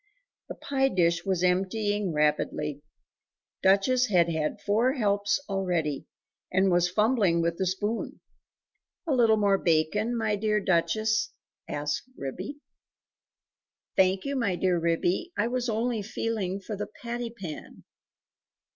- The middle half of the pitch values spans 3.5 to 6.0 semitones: Yes, average, 4.1 semitones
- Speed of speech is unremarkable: No, slow, 130 wpm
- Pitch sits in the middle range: No, high, 200 Hz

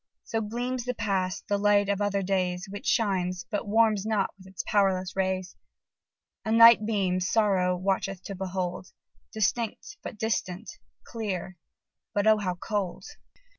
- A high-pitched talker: Yes, high, 200 Hz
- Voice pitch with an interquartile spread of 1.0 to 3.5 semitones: Yes, average, 2.8 semitones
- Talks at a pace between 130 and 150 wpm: Yes, average, 145 wpm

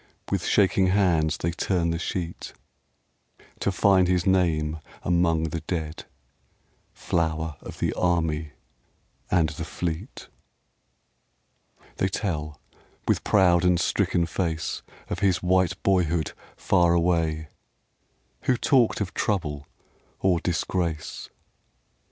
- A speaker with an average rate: No, slow, 110 wpm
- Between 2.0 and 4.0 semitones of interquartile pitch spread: Yes, narrow, 2.4 semitones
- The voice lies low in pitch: Yes, very low, 85 Hz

